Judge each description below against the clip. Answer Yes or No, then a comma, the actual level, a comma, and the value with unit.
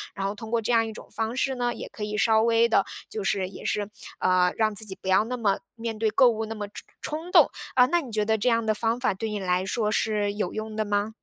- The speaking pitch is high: Yes, high, 220 Hz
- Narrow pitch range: Yes, narrow, 2.0 semitones